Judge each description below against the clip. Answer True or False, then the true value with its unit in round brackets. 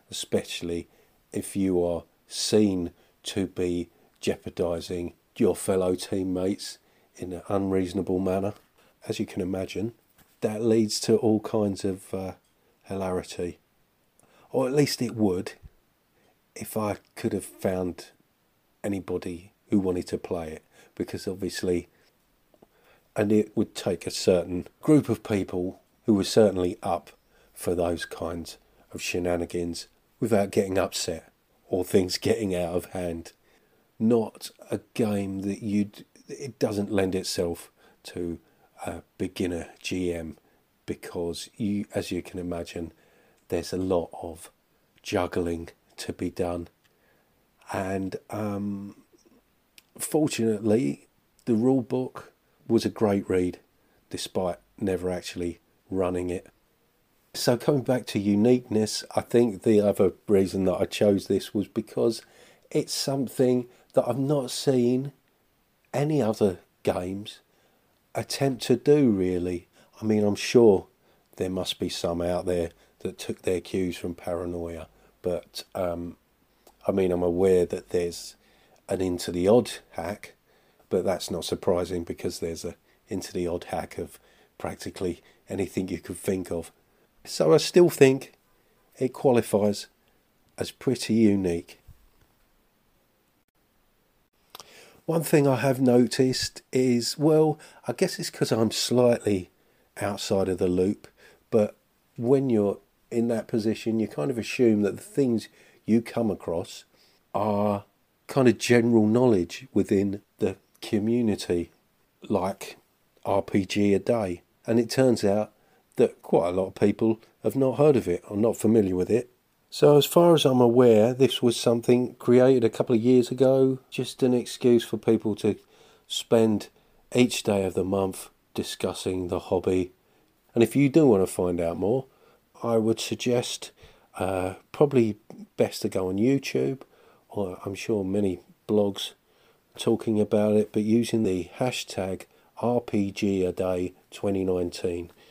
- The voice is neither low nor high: False (105 Hz)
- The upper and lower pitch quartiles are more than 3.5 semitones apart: True (4.5 semitones)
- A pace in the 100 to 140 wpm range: True (135 wpm)